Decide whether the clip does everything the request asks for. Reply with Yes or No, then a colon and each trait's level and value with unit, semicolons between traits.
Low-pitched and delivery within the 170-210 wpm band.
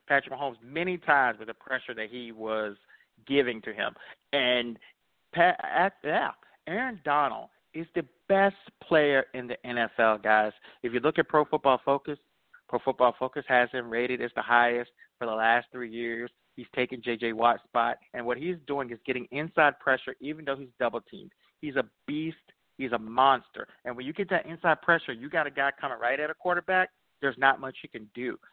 Yes: low, 130 Hz; average, 195 wpm